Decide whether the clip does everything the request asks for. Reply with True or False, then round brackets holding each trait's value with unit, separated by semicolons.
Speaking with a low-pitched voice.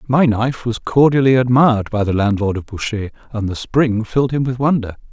True (120 Hz)